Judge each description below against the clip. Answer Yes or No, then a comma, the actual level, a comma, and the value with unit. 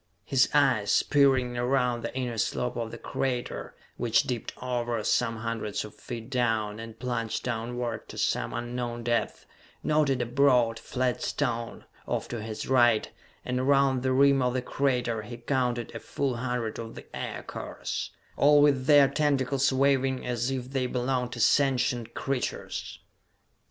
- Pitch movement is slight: Yes, narrow, 2.2 semitones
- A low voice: Yes, low, 125 Hz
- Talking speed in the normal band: Yes, average, 155 wpm